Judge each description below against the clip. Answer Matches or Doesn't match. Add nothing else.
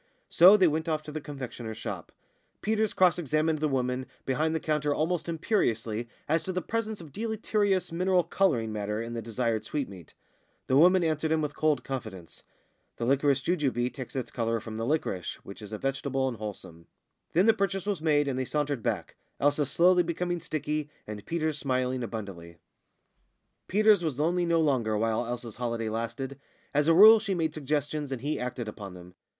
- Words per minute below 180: Doesn't match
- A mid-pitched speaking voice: Matches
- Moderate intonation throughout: Doesn't match